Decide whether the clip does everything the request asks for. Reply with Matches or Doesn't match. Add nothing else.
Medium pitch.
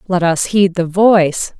Matches